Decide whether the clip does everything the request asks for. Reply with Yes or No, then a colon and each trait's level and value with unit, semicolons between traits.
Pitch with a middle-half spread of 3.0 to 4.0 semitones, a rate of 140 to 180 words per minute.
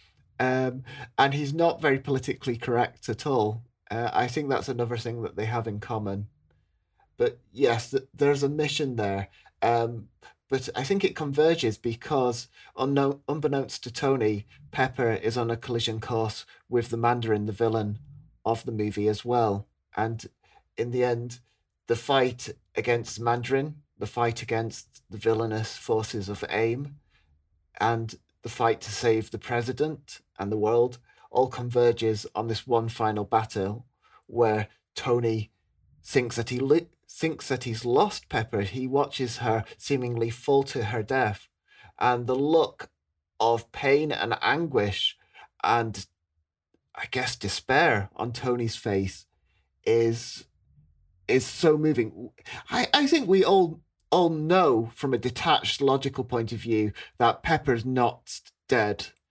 Yes: average, 3.6 semitones; average, 145 wpm